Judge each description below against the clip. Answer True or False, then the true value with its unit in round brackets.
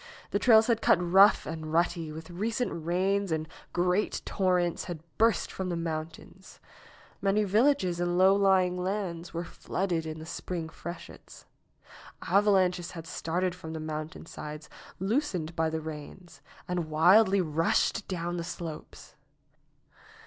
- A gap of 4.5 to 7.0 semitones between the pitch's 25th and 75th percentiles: False (3.0 semitones)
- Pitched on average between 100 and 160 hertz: False (175 Hz)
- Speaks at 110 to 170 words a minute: True (135 wpm)